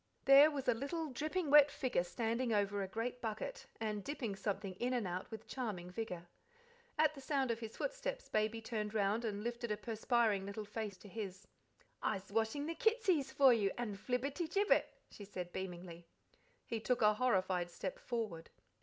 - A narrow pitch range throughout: No, average, 4.8 semitones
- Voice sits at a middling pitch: No, high, 225 Hz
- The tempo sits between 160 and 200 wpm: Yes, average, 180 wpm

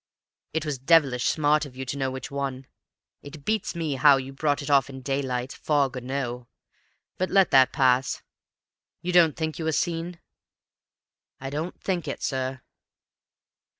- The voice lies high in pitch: No, medium, 140 Hz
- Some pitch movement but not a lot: Yes, average, 3.2 semitones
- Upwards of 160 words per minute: Yes, average, 170 wpm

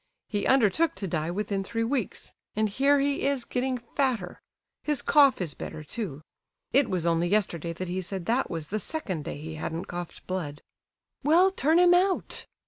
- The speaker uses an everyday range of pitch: No, wide, 8.1 semitones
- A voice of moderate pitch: No, high, 210 Hz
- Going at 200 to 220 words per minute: No, average, 180 wpm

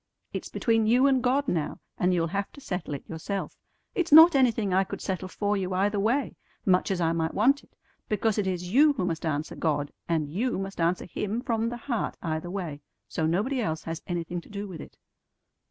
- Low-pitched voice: No, high, 195 Hz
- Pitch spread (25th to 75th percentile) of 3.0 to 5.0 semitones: No, wide, 5.5 semitones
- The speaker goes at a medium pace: No, fast, 215 wpm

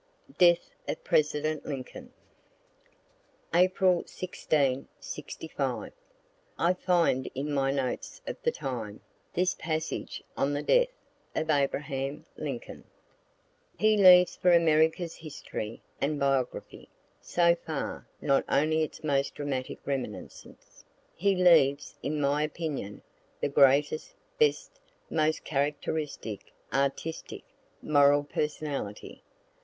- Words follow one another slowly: Yes, slow, 105 wpm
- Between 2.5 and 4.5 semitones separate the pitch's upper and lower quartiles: Yes, average, 3.4 semitones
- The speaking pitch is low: No, medium, 150 Hz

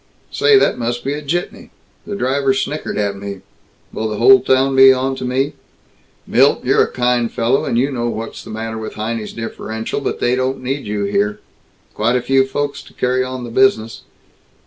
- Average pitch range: Yes, average, 3.3 semitones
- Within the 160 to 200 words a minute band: Yes, average, 195 wpm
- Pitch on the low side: Yes, low, 125 Hz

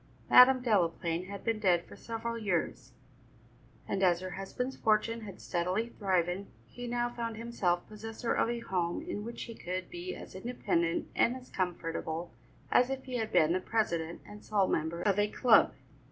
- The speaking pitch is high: Yes, high, 205 Hz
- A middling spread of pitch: Yes, average, 4.9 semitones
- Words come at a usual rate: Yes, average, 175 wpm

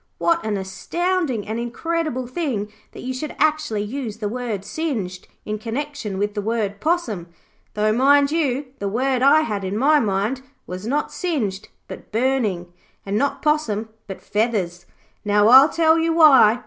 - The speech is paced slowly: No, average, 160 wpm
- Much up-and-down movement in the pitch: Yes, wide, 6.0 semitones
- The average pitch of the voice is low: No, high, 235 Hz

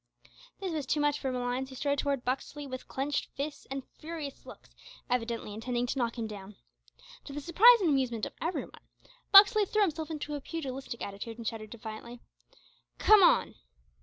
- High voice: Yes, very high, 270 Hz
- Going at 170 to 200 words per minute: Yes, average, 180 wpm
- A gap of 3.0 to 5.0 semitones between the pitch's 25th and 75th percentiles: Yes, average, 4.5 semitones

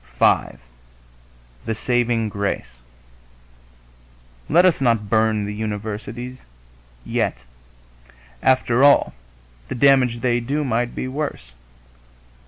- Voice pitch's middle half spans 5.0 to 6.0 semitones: No, average, 3.4 semitones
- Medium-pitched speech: No, low, 120 Hz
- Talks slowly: Yes, slow, 95 wpm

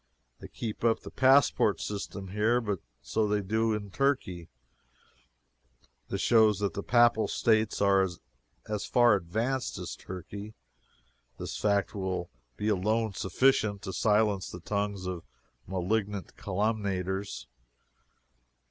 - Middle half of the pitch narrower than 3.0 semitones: Yes, narrow, 2.6 semitones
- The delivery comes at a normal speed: No, slow, 120 wpm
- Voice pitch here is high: No, low, 105 Hz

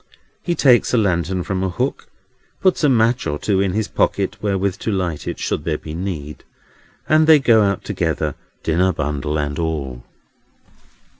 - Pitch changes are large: Yes, wide, 6.0 semitones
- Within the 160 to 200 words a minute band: Yes, average, 170 wpm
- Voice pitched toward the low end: Yes, very low, 95 Hz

